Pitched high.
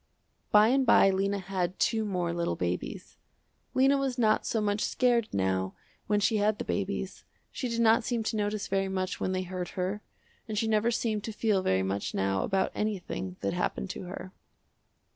Yes: high, 200 Hz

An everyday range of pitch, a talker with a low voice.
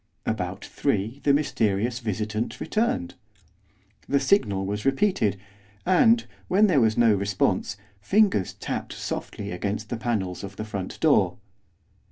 No: wide, 5.9 semitones; low, 110 Hz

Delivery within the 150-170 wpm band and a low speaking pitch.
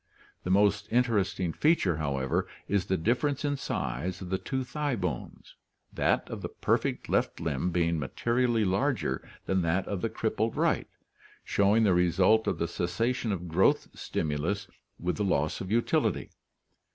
Yes: average, 155 wpm; very low, 95 Hz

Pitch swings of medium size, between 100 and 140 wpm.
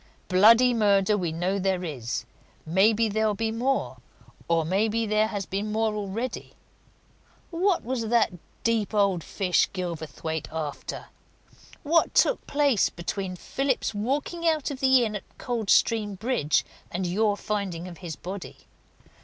Yes: average, 4.0 semitones; slow, 135 wpm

